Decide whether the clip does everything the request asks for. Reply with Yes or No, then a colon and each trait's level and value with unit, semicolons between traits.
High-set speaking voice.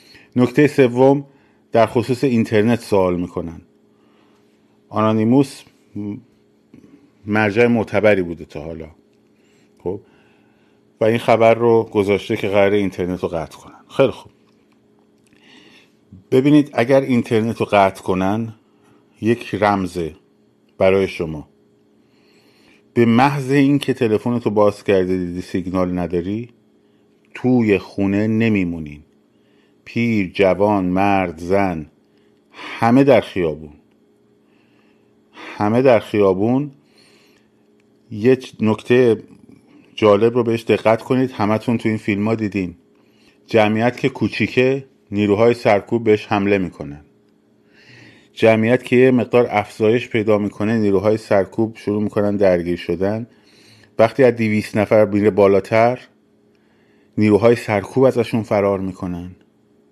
No: low, 105 Hz